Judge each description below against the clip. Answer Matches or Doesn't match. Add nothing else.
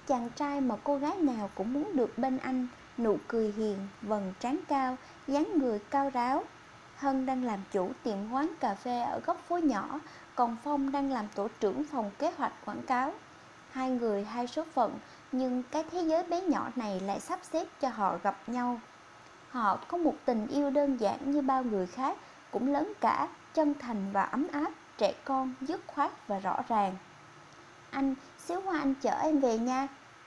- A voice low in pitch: Doesn't match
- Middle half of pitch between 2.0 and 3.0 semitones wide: Doesn't match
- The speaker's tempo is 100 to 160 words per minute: Doesn't match